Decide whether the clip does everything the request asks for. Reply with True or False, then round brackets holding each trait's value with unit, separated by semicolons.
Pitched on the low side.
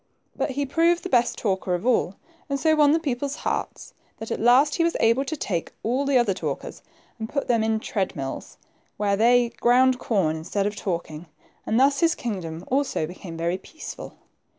False (235 Hz)